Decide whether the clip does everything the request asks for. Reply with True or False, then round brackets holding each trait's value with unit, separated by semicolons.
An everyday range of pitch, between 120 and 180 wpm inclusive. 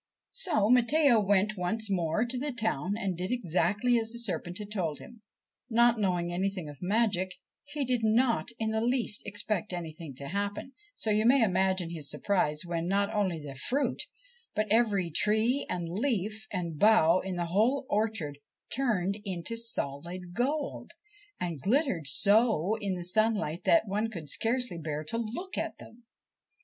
True (4.8 semitones; 165 wpm)